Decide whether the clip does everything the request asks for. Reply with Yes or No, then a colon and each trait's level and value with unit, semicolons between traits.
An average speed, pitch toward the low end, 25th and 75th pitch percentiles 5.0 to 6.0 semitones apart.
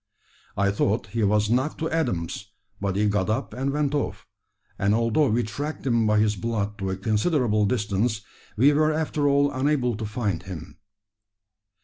Yes: average, 170 wpm; low, 110 Hz; average, 5.3 semitones